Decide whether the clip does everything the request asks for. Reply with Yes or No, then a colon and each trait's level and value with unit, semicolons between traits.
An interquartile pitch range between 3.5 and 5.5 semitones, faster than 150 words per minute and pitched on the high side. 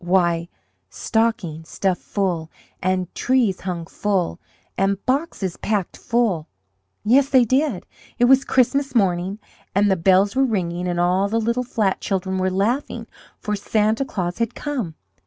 No: average, 4.6 semitones; average, 145 wpm; high, 200 Hz